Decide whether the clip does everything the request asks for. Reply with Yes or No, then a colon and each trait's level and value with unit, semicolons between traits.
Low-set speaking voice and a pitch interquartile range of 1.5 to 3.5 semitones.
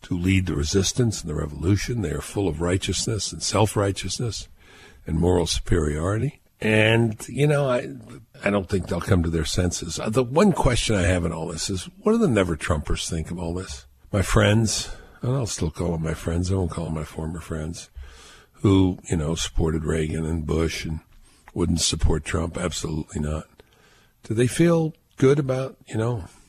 No: very low, 90 Hz; average, 5.3 semitones